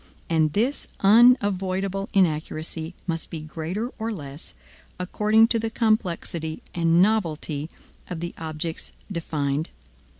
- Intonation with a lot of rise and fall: No, average, 4.9 semitones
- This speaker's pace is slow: Yes, slow, 110 wpm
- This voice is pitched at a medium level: Yes, medium, 175 Hz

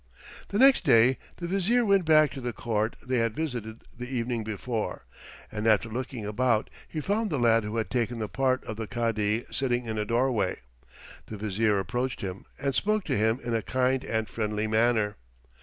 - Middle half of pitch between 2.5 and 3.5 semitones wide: Yes, average, 3.2 semitones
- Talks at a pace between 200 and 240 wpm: No, average, 190 wpm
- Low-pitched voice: Yes, low, 120 Hz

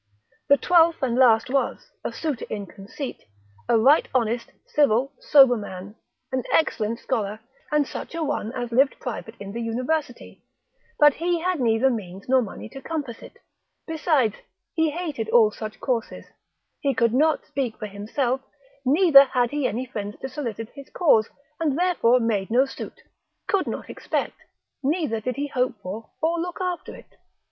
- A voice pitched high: Yes, very high, 255 Hz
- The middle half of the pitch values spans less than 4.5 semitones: No, average, 4.9 semitones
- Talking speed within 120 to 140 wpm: No, average, 165 wpm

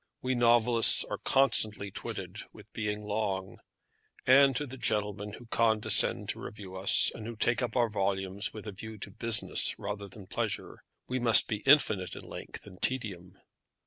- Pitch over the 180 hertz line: No, low, 110 Hz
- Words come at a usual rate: Yes, average, 170 wpm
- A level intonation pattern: No, average, 3.0 semitones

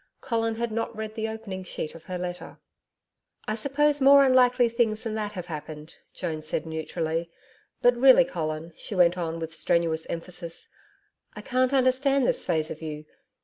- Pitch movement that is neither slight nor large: No, wide, 6.8 semitones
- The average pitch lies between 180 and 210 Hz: Yes, high, 190 Hz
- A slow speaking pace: No, average, 170 wpm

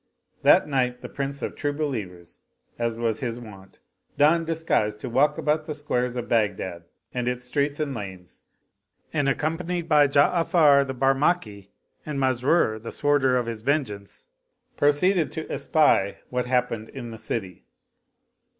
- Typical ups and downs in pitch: Yes, average, 4.7 semitones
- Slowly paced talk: No, average, 150 wpm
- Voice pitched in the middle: No, low, 130 Hz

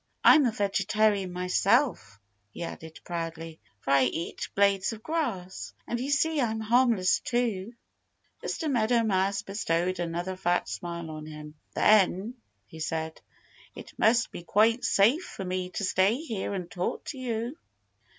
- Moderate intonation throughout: Yes, average, 4.9 semitones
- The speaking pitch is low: No, high, 195 Hz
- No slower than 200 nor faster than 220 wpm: No, average, 150 wpm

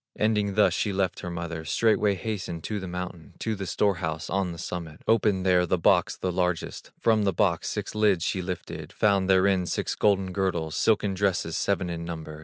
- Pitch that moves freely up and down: No, average, 2.8 semitones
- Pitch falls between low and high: No, very low, 95 Hz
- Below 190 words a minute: No, average, 200 wpm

